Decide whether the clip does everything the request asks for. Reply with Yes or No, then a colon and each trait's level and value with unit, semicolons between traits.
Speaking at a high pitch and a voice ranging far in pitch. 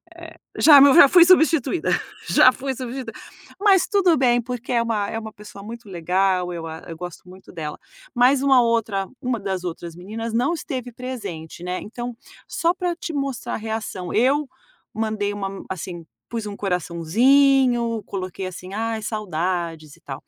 Yes: high, 225 Hz; wide, 5.8 semitones